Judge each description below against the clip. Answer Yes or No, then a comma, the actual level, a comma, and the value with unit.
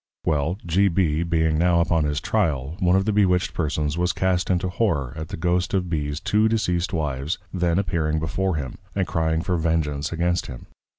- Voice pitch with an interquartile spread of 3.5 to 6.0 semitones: No, average, 2.8 semitones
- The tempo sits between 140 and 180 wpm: No, average, 190 wpm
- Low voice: Yes, very low, 85 Hz